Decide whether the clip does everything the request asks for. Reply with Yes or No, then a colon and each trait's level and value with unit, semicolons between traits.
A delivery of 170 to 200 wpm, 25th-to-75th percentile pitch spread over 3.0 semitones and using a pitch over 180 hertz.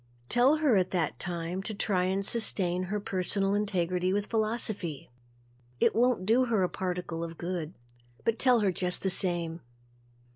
No: average, 160 wpm; average, 3.4 semitones; high, 190 Hz